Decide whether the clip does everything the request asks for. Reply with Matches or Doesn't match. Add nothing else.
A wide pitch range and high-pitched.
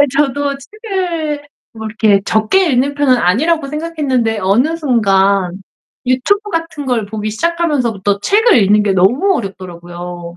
Matches